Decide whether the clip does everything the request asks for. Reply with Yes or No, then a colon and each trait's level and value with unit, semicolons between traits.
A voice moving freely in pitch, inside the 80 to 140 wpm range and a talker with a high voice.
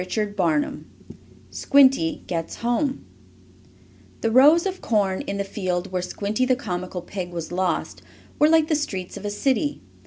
No: wide, 6.6 semitones; average, 155 wpm; high, 205 Hz